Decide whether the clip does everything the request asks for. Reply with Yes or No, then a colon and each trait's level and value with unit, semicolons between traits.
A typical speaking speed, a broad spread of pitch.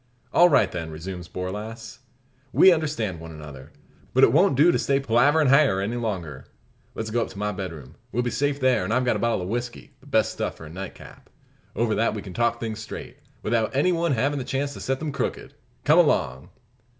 No: fast, 215 wpm; wide, 6.4 semitones